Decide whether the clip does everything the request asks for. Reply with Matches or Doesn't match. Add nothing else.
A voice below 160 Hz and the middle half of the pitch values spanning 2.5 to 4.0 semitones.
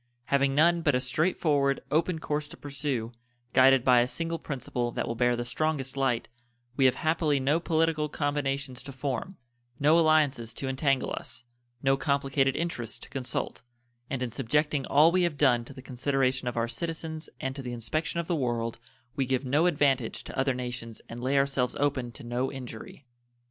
Matches